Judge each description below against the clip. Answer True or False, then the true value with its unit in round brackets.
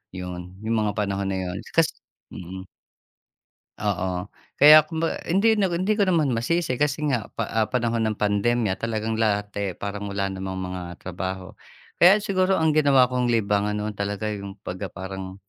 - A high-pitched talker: False (105 Hz)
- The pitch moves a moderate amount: False (6.2 semitones)